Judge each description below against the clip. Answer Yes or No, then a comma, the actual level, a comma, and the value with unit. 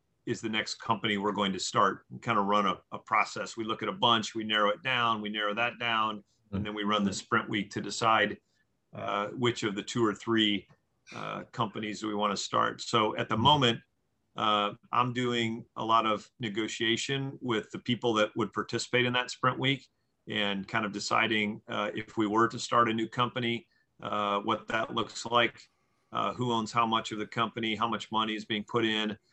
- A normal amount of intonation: No, narrow, 2.0 semitones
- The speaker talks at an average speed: No, fast, 215 wpm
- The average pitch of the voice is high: No, low, 110 Hz